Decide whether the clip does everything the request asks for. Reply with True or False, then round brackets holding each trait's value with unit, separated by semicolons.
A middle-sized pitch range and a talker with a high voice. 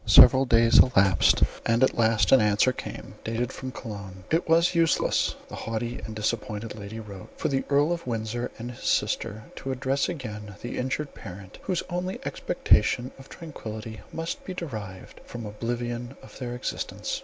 False (3.7 semitones; 120 Hz)